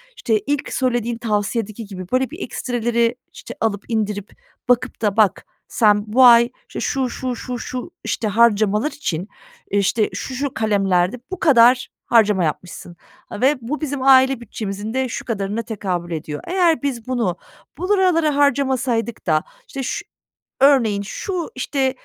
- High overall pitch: Yes, high, 235 Hz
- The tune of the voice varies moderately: Yes, average, 4.3 semitones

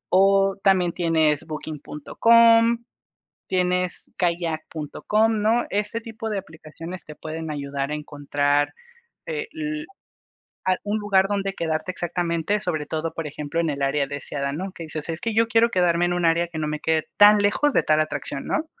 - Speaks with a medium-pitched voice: Yes, medium, 175 Hz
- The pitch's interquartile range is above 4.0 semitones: Yes, average, 5.0 semitones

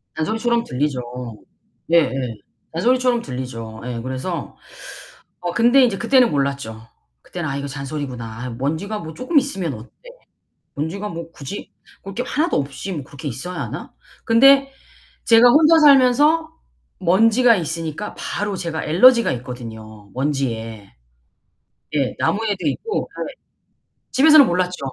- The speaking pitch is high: No, medium, 170 Hz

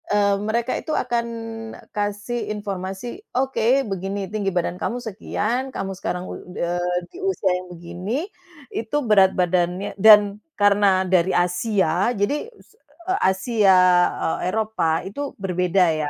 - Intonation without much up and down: No, average, 3.6 semitones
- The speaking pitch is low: No, high, 200 Hz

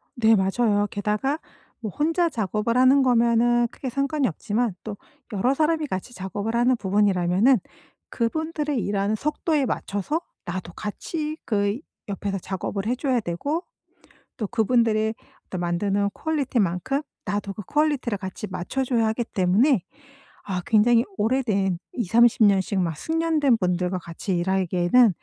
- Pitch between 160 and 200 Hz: No, high, 220 Hz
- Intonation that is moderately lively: Yes, average, 5.0 semitones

